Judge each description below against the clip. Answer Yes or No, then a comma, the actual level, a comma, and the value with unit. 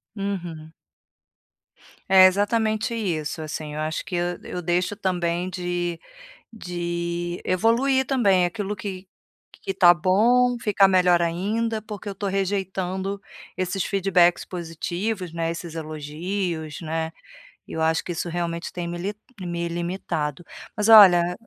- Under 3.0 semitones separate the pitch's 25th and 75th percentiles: Yes, narrow, 2.6 semitones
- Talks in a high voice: No, medium, 180 Hz